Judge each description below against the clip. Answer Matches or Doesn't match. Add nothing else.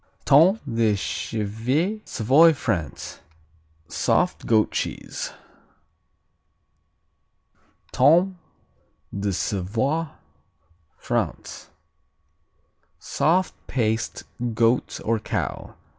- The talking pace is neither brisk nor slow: Doesn't match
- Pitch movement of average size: Doesn't match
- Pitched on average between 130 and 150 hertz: Doesn't match